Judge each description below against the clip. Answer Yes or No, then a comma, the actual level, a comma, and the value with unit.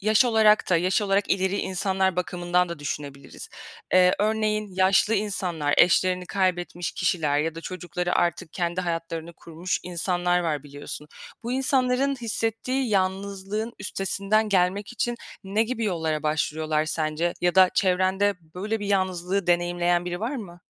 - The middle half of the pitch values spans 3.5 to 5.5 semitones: No, average, 3.0 semitones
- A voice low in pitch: No, medium, 185 Hz